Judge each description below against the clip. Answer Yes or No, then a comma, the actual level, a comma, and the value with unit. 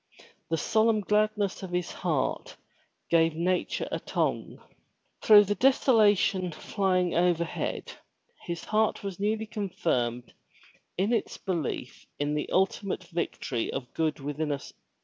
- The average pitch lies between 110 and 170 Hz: No, medium, 185 Hz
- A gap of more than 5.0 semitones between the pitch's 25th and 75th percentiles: No, average, 4.5 semitones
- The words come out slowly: Yes, slow, 130 wpm